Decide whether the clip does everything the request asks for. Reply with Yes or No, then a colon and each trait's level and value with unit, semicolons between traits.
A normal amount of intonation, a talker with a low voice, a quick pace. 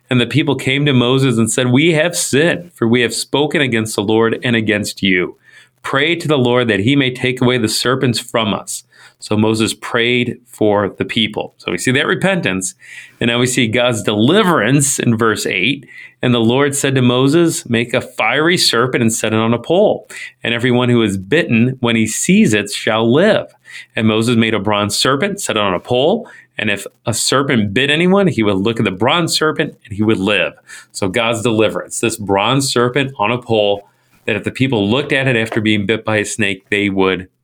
Yes: average, 3.3 semitones; low, 115 Hz; fast, 215 wpm